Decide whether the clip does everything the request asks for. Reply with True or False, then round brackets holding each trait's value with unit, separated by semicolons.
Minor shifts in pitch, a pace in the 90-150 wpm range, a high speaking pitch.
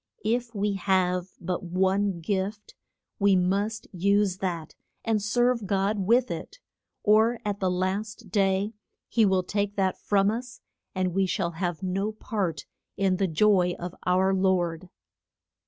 True (2.3 semitones; 145 wpm; 195 Hz)